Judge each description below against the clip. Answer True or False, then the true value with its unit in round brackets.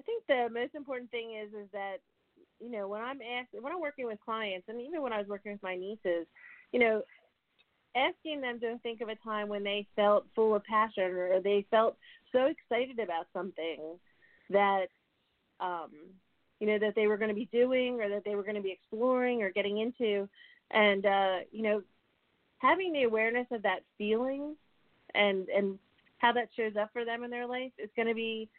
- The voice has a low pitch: False (220 Hz)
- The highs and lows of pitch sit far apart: False (3.3 semitones)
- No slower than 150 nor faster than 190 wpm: False (205 wpm)